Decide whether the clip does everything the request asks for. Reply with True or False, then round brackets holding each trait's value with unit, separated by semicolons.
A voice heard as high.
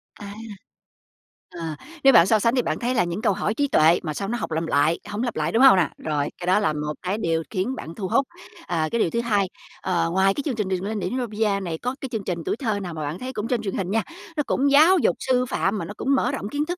True (205 Hz)